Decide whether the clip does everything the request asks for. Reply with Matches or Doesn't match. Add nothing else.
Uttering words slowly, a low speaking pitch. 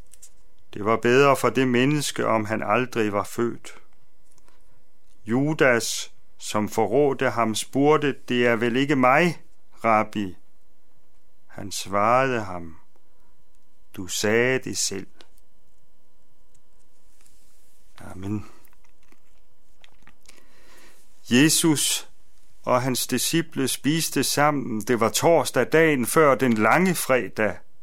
Matches